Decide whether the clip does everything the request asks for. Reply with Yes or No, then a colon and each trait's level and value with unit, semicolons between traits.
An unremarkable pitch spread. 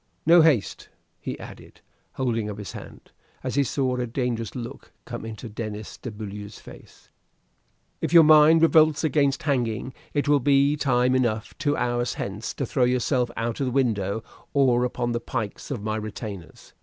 Yes: average, 4.1 semitones